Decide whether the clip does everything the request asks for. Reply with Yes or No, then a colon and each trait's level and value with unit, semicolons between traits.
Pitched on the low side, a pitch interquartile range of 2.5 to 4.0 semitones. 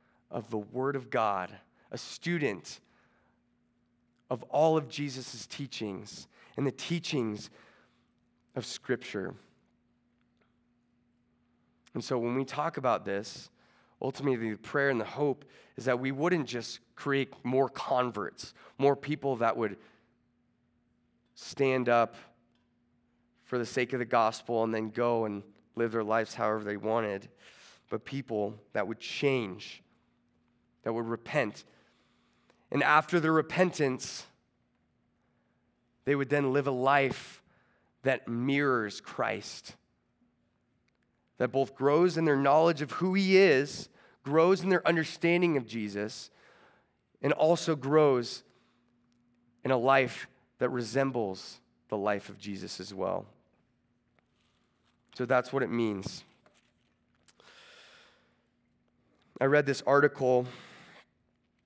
Yes: low, 125 Hz; average, 3.3 semitones